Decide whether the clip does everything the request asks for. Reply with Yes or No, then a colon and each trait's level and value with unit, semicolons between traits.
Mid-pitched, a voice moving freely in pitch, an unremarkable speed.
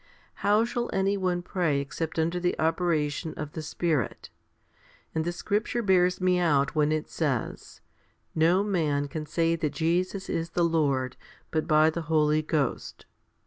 No: medium, 165 Hz; average, 2.7 semitones; average, 155 wpm